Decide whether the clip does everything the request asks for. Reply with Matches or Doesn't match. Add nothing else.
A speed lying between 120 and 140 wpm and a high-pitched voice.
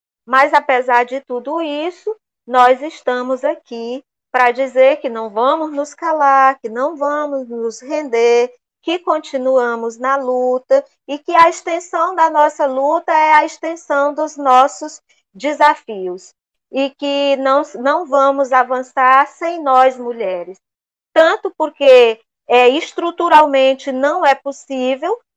Matches